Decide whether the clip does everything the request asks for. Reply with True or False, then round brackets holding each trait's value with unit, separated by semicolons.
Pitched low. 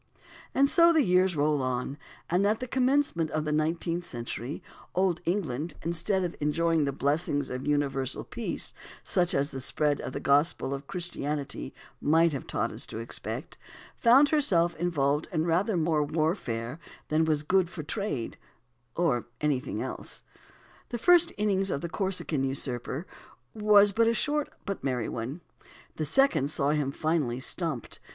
False (160 Hz)